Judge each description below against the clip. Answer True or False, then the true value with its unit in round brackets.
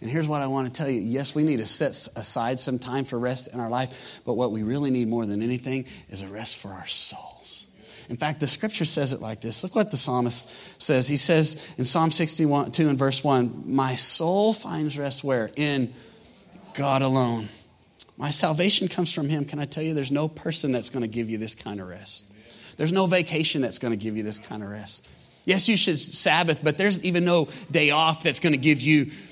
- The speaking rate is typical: False (230 wpm)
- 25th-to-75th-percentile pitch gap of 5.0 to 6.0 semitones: False (4.5 semitones)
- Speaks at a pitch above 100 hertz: True (140 Hz)